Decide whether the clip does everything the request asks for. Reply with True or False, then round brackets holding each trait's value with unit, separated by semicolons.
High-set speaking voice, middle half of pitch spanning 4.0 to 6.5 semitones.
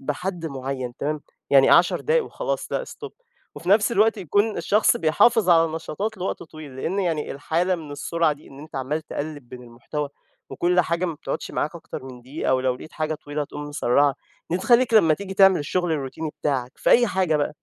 False (155 Hz; 4.6 semitones)